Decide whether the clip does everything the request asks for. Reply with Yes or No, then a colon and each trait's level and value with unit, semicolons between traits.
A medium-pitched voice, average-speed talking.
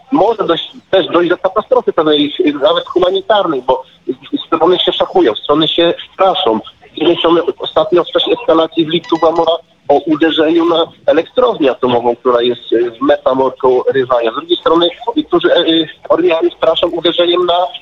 Yes: medium, 175 Hz; average, 140 wpm